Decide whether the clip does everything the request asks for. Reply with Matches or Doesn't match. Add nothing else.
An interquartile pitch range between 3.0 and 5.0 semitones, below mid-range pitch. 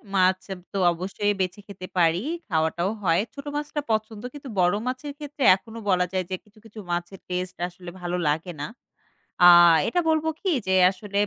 Doesn't match